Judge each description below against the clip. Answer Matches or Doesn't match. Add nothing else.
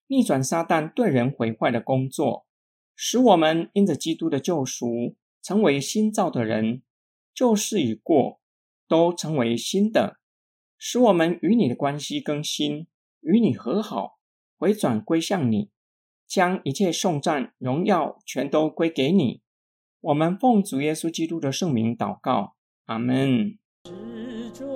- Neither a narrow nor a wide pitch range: Doesn't match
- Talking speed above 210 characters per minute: Doesn't match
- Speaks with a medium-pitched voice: Matches